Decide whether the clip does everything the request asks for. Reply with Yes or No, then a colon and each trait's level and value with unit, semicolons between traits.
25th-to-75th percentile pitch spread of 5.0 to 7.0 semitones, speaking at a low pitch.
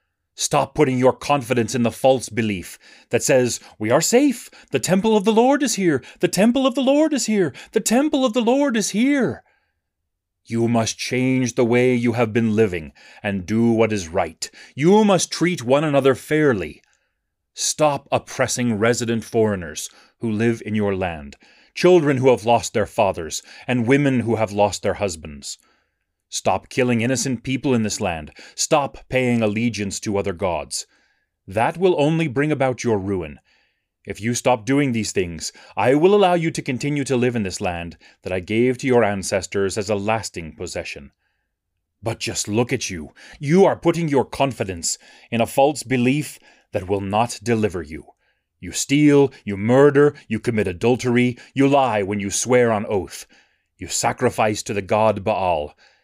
Yes: average, 5.3 semitones; low, 120 Hz